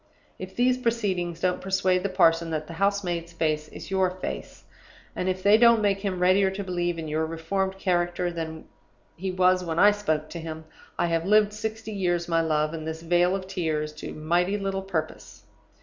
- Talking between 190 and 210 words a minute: Yes, average, 195 wpm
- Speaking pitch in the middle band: Yes, medium, 180 Hz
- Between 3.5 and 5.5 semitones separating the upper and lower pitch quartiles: No, average, 3.0 semitones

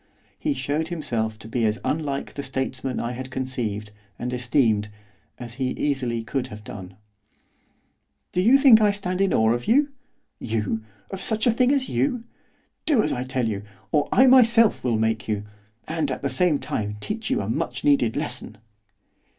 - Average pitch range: No, wide, 8.3 semitones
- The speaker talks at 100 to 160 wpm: No, average, 180 wpm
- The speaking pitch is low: Yes, low, 130 Hz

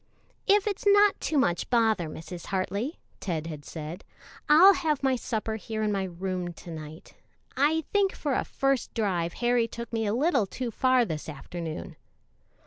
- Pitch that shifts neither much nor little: No, wide, 7.7 semitones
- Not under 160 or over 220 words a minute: Yes, average, 170 wpm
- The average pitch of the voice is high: Yes, high, 220 Hz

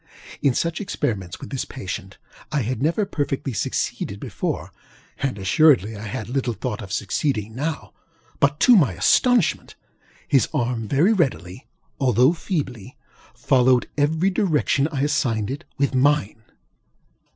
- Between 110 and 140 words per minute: Yes, slow, 135 wpm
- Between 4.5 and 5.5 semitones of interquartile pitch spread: Yes, average, 5.2 semitones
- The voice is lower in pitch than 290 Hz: Yes, low, 135 Hz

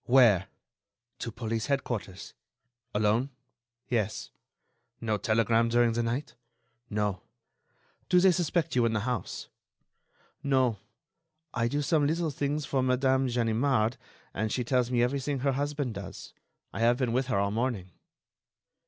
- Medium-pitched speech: No, low, 120 Hz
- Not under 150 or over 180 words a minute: No, slow, 135 wpm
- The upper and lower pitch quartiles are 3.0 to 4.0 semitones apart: Yes, average, 3.4 semitones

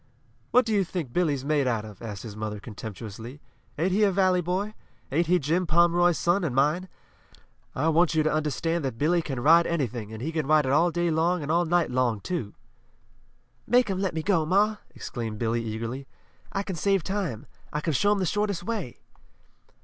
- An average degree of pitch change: No, wide, 5.9 semitones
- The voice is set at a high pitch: No, medium, 160 Hz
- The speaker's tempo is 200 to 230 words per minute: Yes, fast, 205 wpm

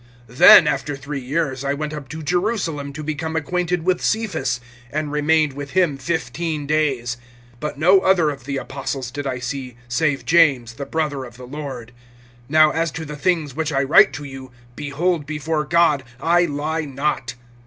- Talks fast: No, average, 175 wpm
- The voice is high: No, medium, 150 Hz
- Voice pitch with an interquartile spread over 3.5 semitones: No, average, 2.9 semitones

